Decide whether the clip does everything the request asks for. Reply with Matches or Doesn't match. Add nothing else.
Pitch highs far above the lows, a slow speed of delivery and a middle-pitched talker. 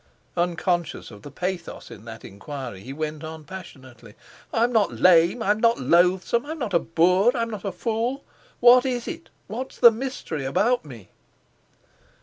Doesn't match